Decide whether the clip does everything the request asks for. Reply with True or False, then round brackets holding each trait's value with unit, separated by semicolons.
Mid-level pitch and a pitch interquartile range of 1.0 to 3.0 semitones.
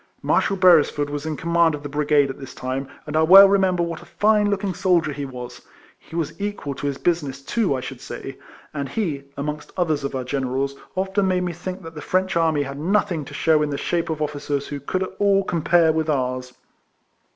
False (155 Hz; 4.5 semitones)